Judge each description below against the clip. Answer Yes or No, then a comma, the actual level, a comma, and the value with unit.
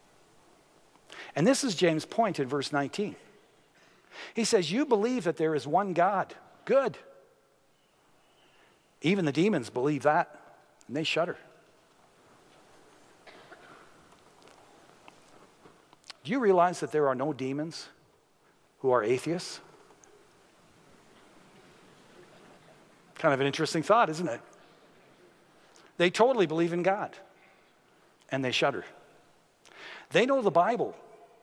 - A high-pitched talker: No, medium, 175 Hz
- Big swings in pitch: Yes, wide, 6.7 semitones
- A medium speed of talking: No, slow, 105 wpm